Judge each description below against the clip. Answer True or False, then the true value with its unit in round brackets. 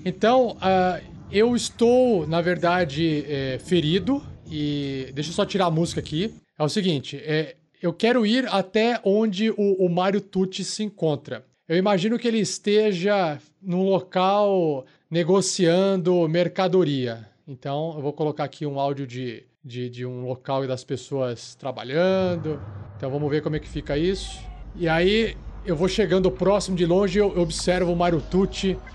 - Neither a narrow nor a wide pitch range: True (4.8 semitones)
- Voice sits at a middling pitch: True (175 Hz)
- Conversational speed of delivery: True (160 wpm)